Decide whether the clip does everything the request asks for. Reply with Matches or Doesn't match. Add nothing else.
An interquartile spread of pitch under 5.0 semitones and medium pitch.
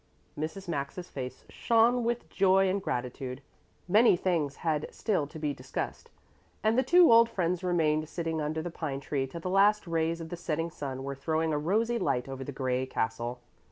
Doesn't match